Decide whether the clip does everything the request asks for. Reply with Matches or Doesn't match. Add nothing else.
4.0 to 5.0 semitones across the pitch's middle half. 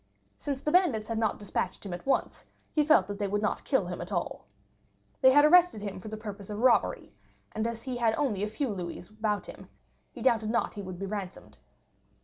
Matches